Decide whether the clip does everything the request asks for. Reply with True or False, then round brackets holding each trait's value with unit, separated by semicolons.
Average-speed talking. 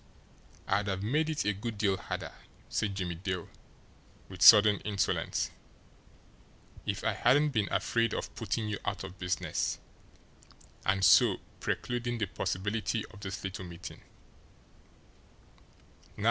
False (125 wpm)